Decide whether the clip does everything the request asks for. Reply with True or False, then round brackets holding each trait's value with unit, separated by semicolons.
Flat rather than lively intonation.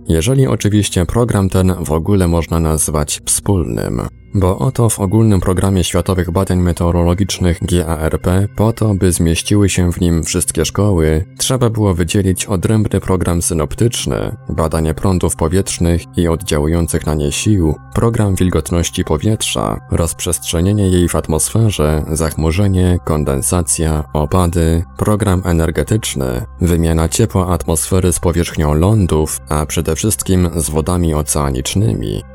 False (3.7 semitones)